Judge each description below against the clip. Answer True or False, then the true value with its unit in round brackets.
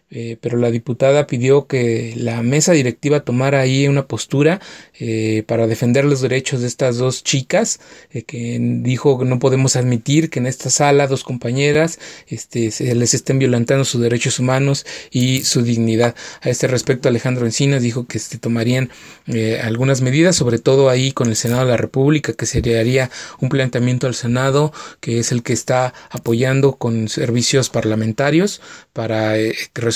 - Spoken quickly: False (175 wpm)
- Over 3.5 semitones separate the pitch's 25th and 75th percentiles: False (2.6 semitones)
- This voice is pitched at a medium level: False (125 Hz)